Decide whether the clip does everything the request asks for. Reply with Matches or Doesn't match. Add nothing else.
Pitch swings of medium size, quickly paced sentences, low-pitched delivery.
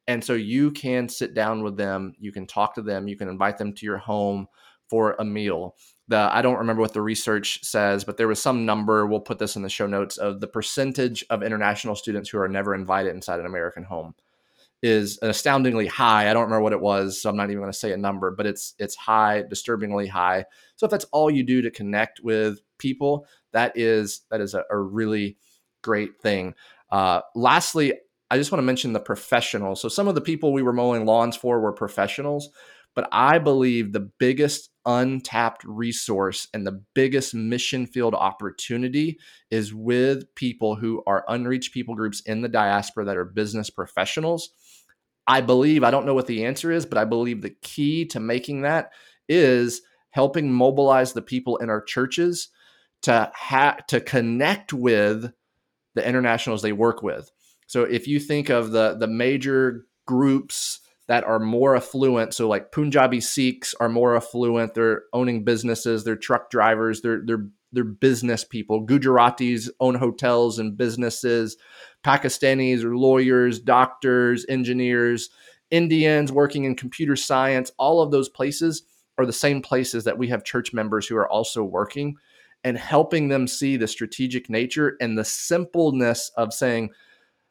Doesn't match